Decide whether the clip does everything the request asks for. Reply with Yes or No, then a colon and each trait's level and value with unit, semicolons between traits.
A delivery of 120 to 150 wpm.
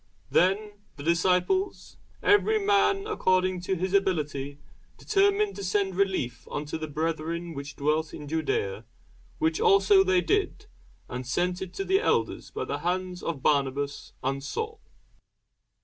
Yes: average, 140 wpm